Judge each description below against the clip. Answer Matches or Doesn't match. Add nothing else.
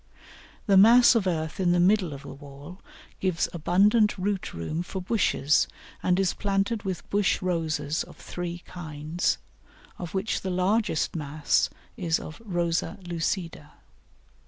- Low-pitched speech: Doesn't match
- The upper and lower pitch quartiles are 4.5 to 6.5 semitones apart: Doesn't match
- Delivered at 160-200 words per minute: Doesn't match